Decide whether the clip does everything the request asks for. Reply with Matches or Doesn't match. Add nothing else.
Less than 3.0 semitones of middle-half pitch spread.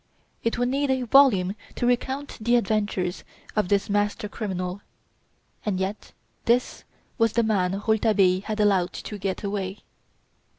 Doesn't match